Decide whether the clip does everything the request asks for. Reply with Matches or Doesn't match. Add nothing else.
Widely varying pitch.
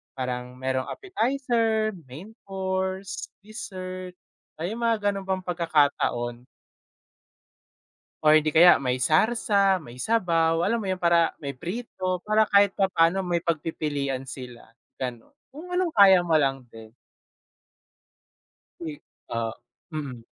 Matches